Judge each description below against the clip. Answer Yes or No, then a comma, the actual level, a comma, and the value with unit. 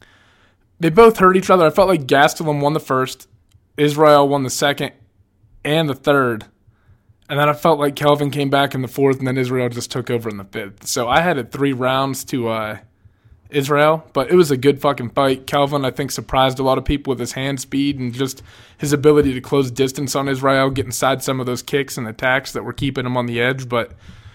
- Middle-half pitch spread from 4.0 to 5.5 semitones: No, average, 3.2 semitones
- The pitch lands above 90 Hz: Yes, low, 135 Hz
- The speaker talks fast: Yes, fast, 225 wpm